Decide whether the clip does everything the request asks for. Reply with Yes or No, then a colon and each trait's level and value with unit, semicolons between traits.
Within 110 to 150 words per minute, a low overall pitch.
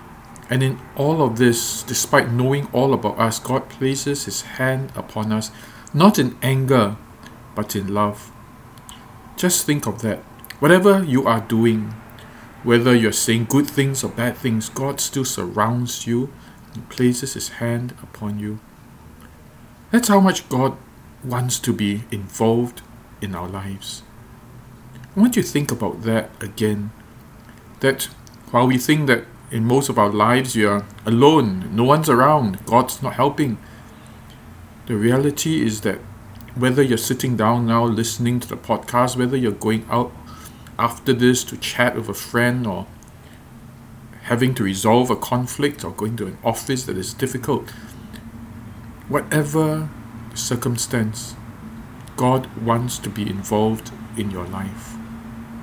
Yes: average, 145 wpm; low, 120 Hz